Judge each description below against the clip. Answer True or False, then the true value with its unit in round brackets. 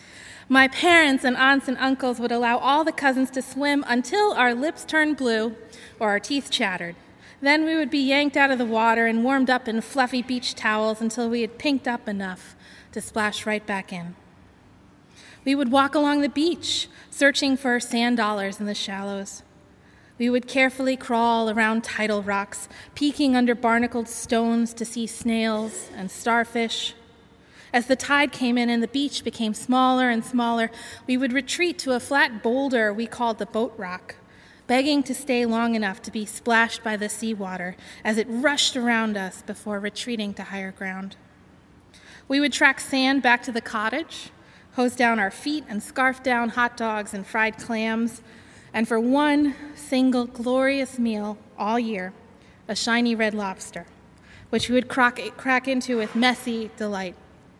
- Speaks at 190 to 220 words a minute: False (170 wpm)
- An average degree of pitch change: True (3.2 semitones)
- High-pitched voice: True (235 Hz)